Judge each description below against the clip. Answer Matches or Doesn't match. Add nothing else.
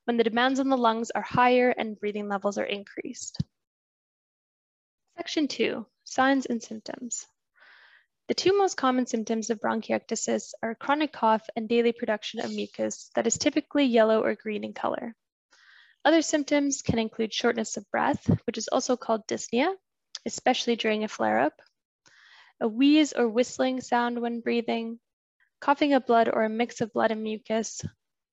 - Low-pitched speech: Doesn't match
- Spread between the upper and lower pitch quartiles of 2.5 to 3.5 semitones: Matches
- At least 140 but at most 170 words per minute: Matches